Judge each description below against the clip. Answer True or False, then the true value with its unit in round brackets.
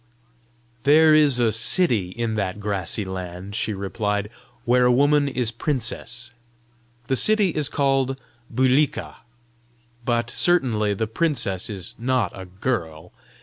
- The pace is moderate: False (125 wpm)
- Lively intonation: False (5.0 semitones)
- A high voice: False (120 Hz)